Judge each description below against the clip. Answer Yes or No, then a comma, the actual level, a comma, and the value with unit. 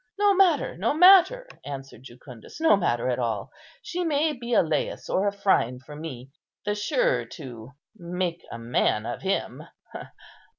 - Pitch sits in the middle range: Yes, medium, 180 Hz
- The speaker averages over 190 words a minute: No, average, 155 wpm